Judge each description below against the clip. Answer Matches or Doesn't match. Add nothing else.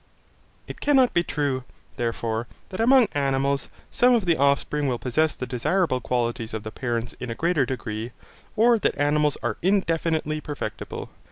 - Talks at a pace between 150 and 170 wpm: Matches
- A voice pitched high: Doesn't match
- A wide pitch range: Matches